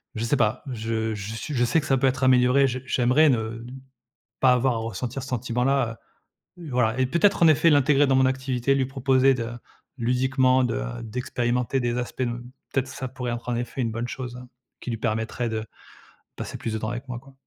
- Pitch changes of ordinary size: No, narrow, 2.1 semitones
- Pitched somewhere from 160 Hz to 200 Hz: No, low, 125 Hz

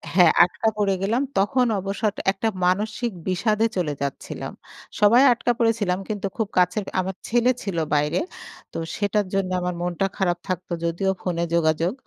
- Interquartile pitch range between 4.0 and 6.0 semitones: No, average, 3.3 semitones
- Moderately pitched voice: No, high, 195 Hz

